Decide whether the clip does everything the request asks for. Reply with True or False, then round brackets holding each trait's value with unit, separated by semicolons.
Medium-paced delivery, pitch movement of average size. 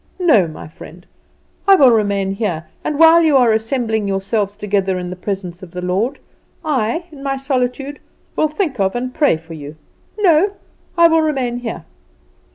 False (170 wpm; 7.1 semitones)